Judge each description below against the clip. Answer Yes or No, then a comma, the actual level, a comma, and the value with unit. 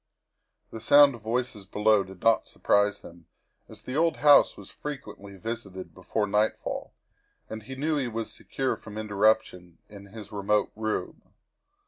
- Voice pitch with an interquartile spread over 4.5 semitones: No, average, 3.0 semitones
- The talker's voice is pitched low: Yes, low, 110 Hz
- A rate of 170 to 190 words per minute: No, average, 150 wpm